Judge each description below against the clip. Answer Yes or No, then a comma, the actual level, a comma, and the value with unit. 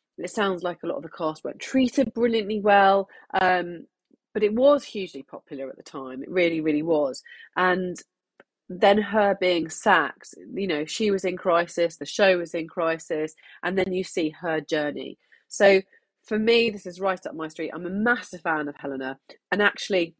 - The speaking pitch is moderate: Yes, medium, 180 Hz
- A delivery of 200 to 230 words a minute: No, average, 185 wpm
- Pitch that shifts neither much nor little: Yes, average, 4.1 semitones